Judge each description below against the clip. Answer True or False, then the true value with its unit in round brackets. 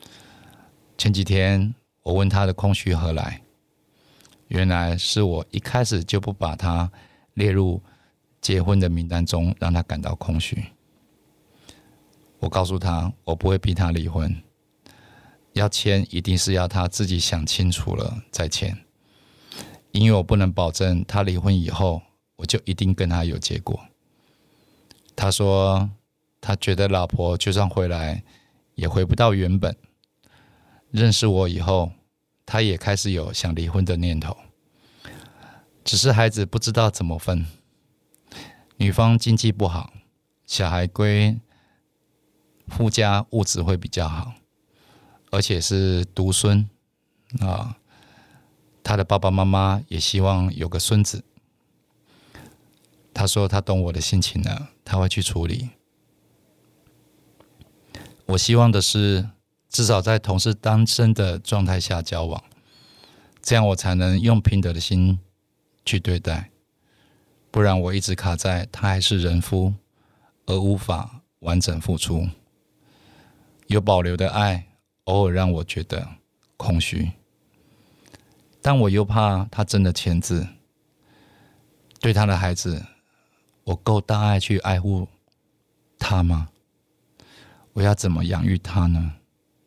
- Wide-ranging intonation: False (2.8 semitones)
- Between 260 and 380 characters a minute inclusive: False (180 characters per minute)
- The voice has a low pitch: True (95 Hz)